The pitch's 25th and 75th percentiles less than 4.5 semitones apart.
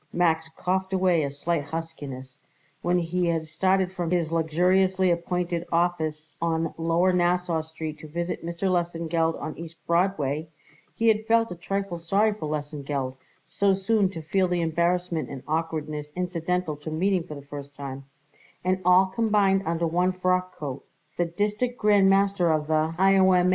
Yes: average, 2.8 semitones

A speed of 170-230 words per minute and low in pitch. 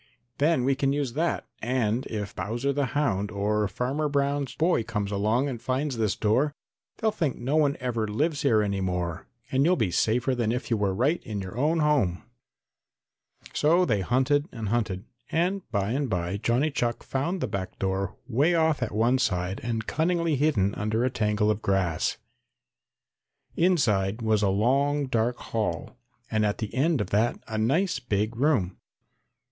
Yes: average, 175 wpm; low, 120 Hz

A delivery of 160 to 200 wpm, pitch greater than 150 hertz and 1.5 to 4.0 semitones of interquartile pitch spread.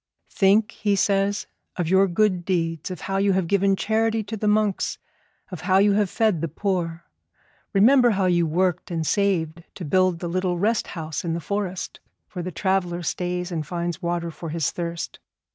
Yes: average, 185 wpm; medium, 185 Hz; average, 2.8 semitones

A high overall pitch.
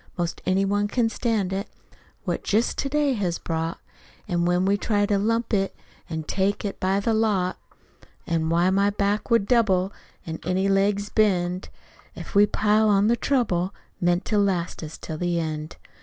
Yes: high, 195 Hz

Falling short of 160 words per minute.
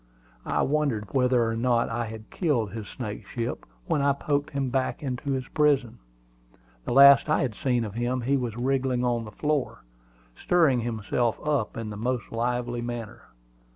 No: average, 170 wpm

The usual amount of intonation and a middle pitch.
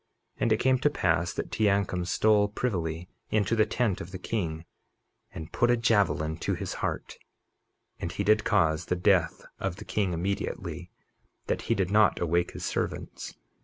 No: average, 3.9 semitones; very low, 95 Hz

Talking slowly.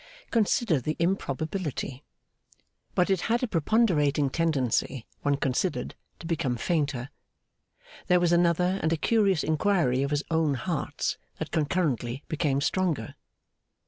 Yes: slow, 125 wpm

